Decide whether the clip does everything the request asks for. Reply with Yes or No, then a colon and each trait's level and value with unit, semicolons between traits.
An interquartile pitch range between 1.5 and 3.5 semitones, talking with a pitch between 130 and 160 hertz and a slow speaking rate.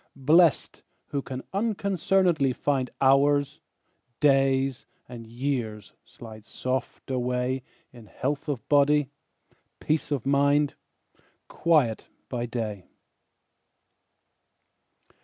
Yes: average, 2.8 semitones; low, 135 Hz; slow, 85 wpm